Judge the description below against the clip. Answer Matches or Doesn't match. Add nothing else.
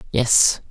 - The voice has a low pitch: Matches